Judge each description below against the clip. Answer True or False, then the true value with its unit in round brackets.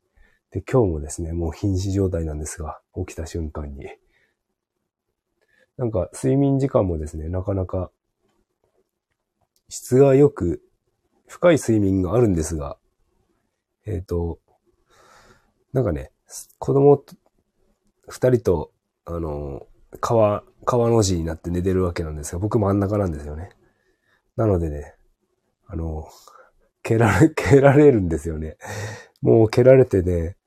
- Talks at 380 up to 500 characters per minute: False (235 characters per minute)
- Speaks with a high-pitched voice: False (95 Hz)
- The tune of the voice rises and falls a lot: True (6.2 semitones)